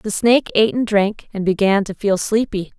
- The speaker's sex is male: No, female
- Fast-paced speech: Yes, fast, 215 wpm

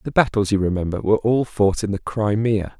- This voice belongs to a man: Yes, male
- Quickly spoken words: Yes, fast, 215 wpm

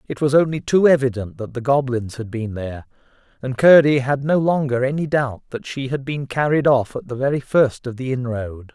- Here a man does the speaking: Yes, male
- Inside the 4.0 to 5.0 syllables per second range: No, 5.3 syllables/s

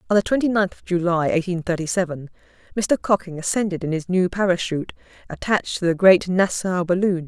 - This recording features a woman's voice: Yes, female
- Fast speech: No, average, 180 wpm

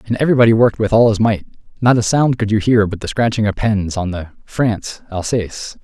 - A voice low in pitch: Yes, low, 110 Hz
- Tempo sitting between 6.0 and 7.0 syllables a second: Yes, 6.2 syllables/s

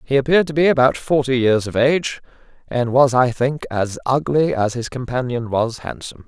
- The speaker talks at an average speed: Yes, average, 190 wpm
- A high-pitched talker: No, low, 130 Hz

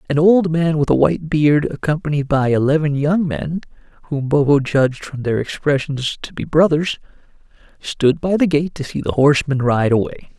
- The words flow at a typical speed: Yes, average, 175 wpm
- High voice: No, medium, 150 Hz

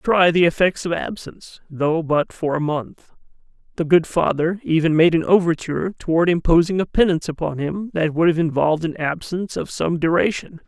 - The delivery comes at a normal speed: Yes, average, 180 wpm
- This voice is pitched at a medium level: Yes, medium, 165 Hz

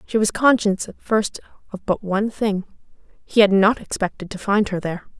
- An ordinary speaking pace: Yes, average, 185 wpm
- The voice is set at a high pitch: Yes, high, 205 Hz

